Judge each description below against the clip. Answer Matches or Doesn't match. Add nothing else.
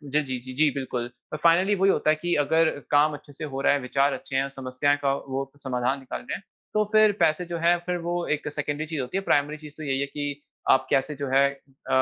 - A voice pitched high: Doesn't match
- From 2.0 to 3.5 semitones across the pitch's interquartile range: Matches